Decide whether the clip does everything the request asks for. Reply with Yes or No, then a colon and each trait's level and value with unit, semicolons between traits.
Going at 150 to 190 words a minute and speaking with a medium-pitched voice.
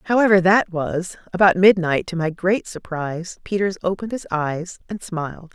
Yes: average, 160 wpm; medium, 180 Hz